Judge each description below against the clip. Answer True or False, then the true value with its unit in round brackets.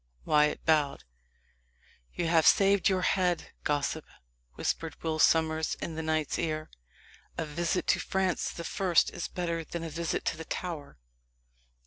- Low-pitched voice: False (165 Hz)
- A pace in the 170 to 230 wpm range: False (145 wpm)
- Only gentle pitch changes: True (1.8 semitones)